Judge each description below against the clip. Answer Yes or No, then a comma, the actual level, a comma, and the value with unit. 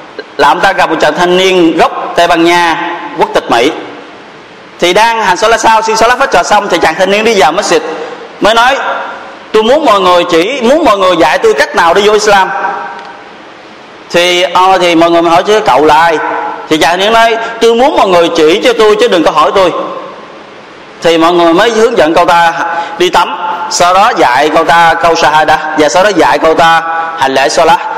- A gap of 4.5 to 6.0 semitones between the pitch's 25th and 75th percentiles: Yes, average, 4.9 semitones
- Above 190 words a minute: Yes, average, 225 wpm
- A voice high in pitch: No, medium, 175 Hz